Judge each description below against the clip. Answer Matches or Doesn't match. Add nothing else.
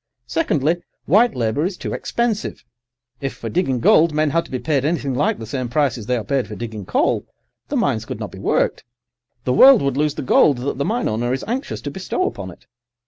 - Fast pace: Matches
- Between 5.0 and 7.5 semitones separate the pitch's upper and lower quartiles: Matches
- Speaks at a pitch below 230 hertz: Matches